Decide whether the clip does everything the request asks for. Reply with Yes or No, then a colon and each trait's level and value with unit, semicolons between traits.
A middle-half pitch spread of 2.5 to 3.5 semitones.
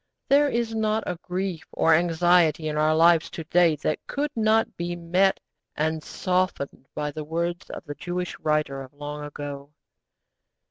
Yes: average, 3.2 semitones